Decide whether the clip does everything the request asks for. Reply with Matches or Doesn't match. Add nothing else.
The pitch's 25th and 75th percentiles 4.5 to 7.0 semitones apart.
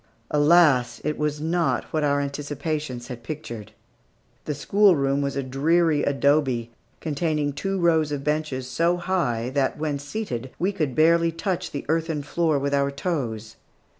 Doesn't match